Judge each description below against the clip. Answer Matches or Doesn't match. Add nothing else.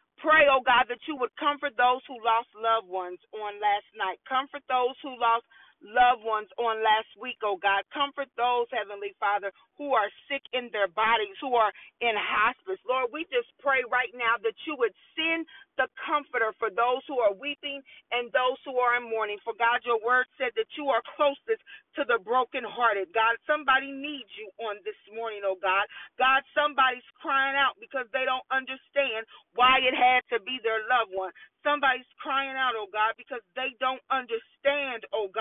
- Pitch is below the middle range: Doesn't match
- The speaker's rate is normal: Matches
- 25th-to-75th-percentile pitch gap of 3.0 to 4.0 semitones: Matches